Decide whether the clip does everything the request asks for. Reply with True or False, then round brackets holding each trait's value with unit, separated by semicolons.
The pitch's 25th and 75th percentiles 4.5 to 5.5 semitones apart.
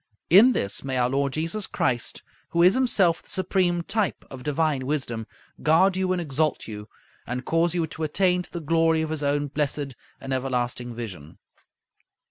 True (4.9 semitones)